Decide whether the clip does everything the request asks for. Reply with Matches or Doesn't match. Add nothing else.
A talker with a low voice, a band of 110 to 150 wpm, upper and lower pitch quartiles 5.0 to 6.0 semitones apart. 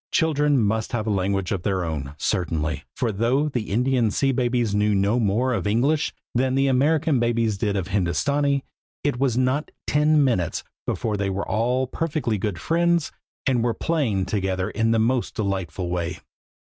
Doesn't match